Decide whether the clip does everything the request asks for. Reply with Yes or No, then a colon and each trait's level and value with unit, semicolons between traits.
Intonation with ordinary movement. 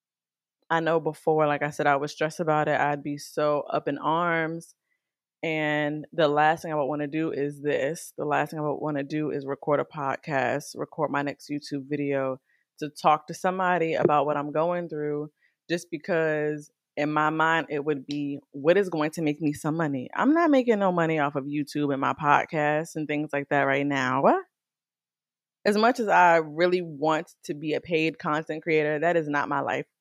No: narrow, 2.0 semitones